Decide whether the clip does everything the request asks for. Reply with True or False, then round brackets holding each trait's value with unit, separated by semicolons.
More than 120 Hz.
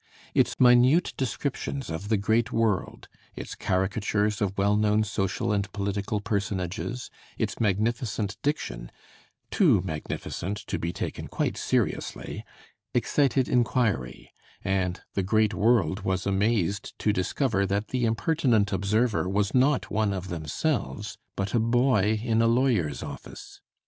False (105 Hz)